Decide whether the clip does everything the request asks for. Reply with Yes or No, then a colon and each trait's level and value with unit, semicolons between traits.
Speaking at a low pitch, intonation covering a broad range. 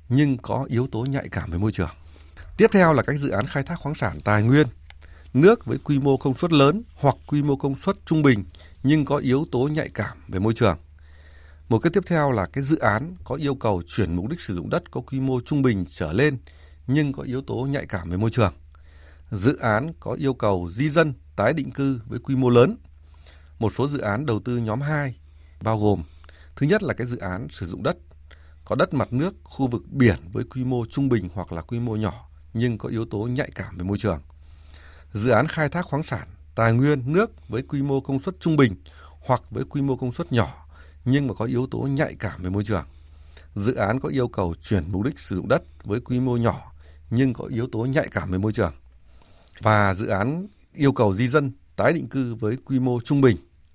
Yes: low, 115 Hz; wide, 7.9 semitones